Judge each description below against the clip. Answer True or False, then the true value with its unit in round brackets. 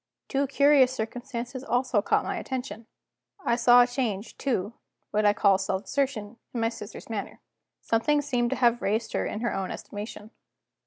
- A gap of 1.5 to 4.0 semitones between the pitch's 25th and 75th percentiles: True (3.5 semitones)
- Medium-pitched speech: False (235 Hz)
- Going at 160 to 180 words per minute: True (170 wpm)